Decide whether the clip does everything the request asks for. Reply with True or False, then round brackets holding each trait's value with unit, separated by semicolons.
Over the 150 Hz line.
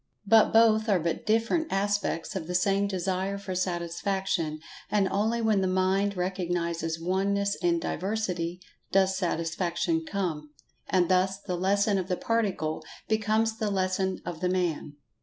True (190 Hz)